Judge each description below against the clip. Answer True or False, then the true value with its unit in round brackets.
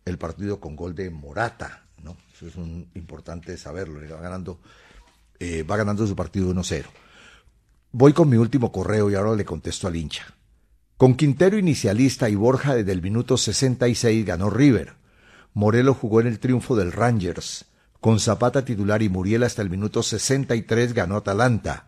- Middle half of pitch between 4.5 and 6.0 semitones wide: True (5.0 semitones)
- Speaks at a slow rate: False (165 wpm)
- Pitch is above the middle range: False (105 Hz)